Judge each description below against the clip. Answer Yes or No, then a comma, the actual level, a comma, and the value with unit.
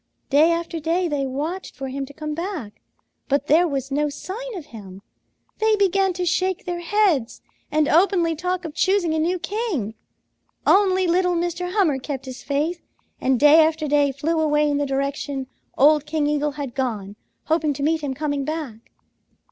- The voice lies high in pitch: Yes, very high, 310 Hz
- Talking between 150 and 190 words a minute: Yes, average, 180 wpm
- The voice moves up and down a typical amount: Yes, average, 4.0 semitones